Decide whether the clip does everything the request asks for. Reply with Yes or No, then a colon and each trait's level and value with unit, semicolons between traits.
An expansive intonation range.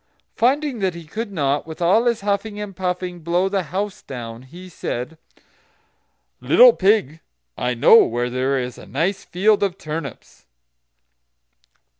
Yes: wide, 6.6 semitones